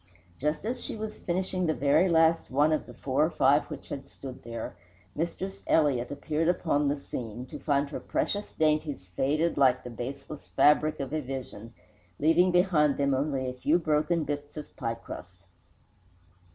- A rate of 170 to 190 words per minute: Yes, average, 175 wpm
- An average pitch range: Yes, average, 3.6 semitones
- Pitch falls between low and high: Yes, medium, 145 Hz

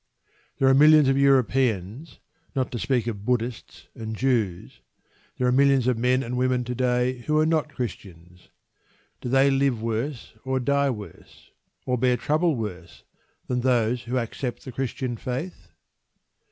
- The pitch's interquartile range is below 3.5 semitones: Yes, narrow, 2.6 semitones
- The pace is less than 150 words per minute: No, average, 155 wpm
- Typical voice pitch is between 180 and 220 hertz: No, low, 125 Hz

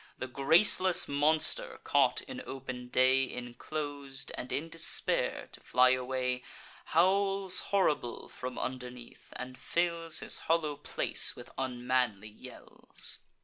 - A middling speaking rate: No, slow, 115 wpm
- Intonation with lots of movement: No, average, 4.7 semitones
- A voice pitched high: No, low, 135 Hz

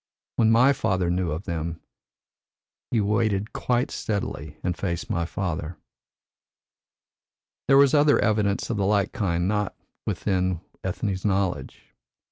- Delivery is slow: Yes, slow, 125 wpm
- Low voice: Yes, low, 100 Hz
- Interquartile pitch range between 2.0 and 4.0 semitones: Yes, average, 3.7 semitones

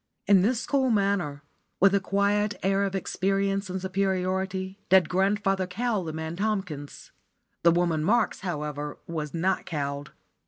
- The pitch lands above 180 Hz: Yes, high, 190 Hz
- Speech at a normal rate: Yes, average, 145 wpm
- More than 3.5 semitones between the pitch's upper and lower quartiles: No, average, 3.0 semitones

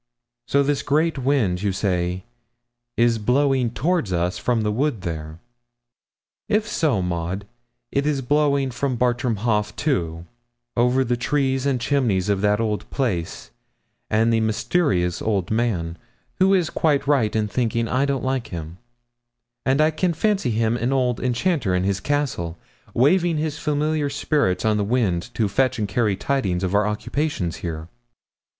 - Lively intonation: Yes, wide, 6.1 semitones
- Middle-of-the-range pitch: No, low, 120 Hz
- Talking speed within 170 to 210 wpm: No, average, 155 wpm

